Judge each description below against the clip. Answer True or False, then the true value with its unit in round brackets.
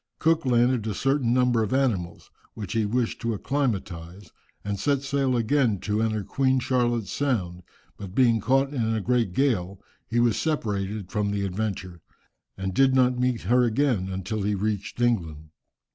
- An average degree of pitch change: True (4.3 semitones)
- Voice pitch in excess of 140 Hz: False (115 Hz)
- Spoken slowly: False (165 wpm)